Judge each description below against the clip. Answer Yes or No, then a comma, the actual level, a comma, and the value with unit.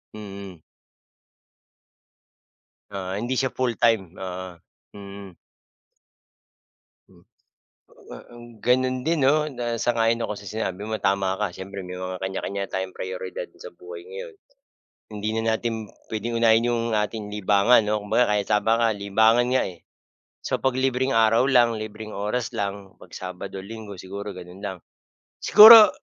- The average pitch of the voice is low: Yes, low, 110 Hz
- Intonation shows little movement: No, average, 3.5 semitones